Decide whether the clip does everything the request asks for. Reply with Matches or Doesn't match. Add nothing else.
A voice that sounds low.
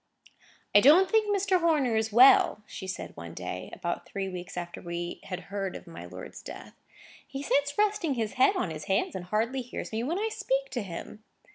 Doesn't match